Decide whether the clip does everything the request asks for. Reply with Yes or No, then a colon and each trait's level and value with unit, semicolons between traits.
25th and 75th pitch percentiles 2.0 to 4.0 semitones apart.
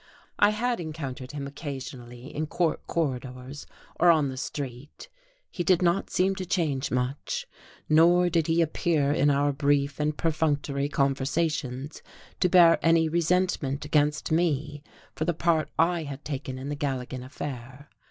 Yes: average, 3.3 semitones